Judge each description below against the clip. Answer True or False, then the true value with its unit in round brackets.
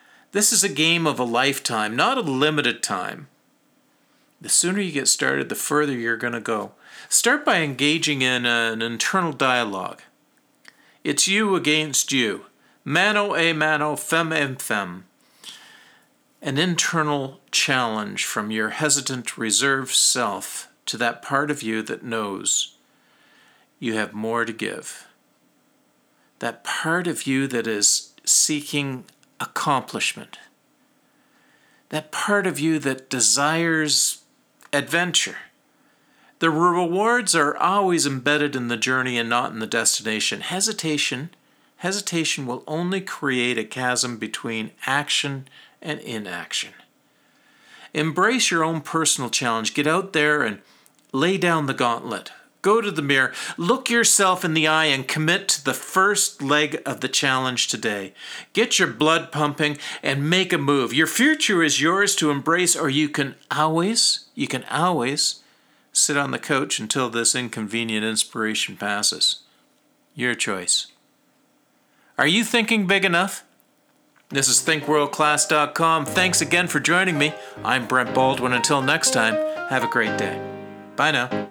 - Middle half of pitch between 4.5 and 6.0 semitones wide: True (5.3 semitones)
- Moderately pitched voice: True (150 Hz)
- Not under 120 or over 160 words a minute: True (140 wpm)